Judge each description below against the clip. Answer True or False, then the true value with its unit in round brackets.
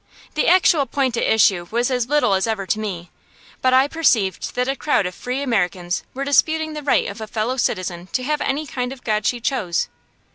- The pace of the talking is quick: True (215 wpm)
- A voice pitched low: False (245 Hz)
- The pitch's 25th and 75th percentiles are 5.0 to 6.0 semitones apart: True (5.6 semitones)